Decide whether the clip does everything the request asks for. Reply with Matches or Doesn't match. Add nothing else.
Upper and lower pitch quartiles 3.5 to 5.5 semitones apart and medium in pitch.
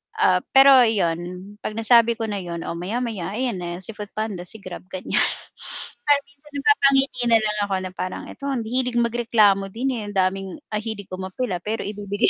Doesn't match